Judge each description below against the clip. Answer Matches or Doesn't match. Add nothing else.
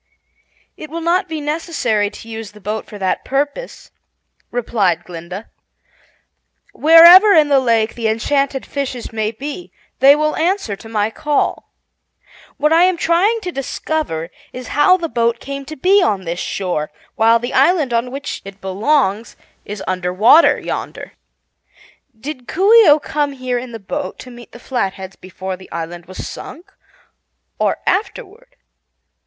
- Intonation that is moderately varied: Doesn't match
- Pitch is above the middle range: Matches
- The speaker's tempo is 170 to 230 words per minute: Doesn't match